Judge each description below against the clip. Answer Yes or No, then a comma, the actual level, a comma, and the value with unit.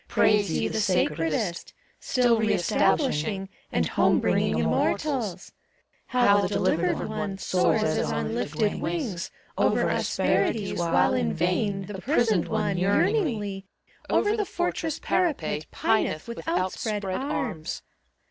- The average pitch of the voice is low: No, high, 200 Hz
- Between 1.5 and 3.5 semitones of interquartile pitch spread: No, average, 4.3 semitones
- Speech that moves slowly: Yes, slow, 120 wpm